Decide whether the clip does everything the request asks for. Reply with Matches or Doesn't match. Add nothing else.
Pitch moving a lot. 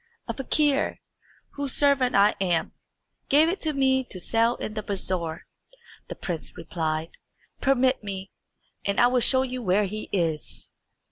Matches